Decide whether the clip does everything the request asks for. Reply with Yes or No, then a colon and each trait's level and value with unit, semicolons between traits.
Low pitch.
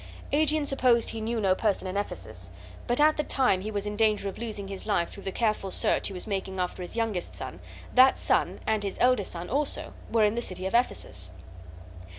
No: high, 210 Hz